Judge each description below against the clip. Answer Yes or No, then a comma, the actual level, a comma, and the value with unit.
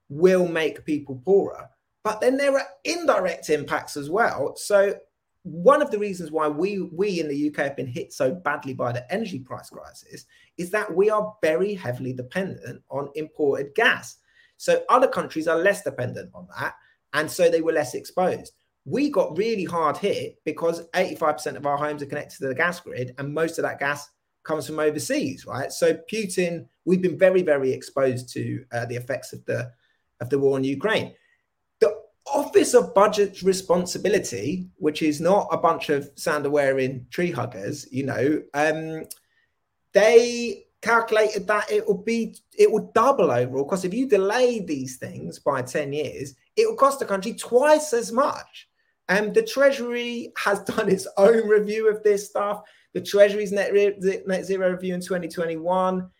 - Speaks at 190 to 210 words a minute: No, average, 180 wpm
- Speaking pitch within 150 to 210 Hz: Yes, medium, 185 Hz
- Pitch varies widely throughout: Yes, wide, 6.2 semitones